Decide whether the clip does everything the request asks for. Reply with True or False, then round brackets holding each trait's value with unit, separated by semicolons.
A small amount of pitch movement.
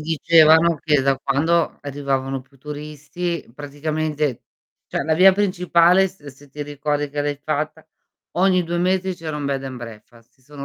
False (3.1 semitones)